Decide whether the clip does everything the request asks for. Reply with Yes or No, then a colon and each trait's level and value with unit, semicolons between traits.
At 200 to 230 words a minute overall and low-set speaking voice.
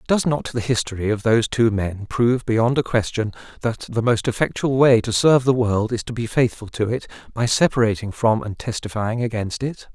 Yes: fast, 205 wpm; low, 115 Hz